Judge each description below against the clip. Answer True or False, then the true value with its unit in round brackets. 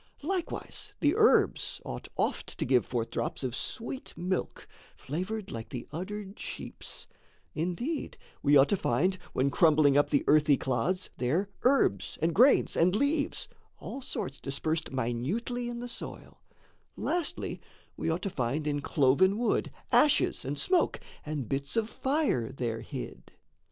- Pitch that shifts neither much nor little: False (8.9 semitones)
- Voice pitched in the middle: True (160 Hz)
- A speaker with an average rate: True (145 wpm)